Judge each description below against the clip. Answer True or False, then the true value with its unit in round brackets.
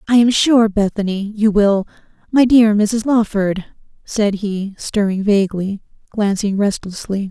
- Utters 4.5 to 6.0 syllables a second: False (4.1 syllables/s)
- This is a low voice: False (210 Hz)